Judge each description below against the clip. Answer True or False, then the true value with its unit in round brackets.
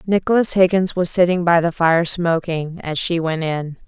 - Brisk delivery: False (185 wpm)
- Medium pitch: True (170 Hz)